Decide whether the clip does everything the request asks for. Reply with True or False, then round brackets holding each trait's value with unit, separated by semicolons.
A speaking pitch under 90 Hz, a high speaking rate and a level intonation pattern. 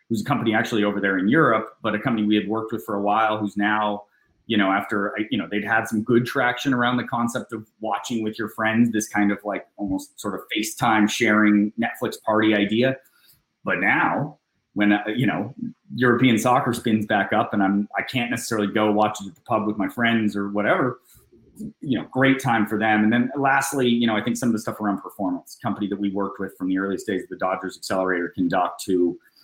False (105 Hz; 225 wpm; 2.3 semitones)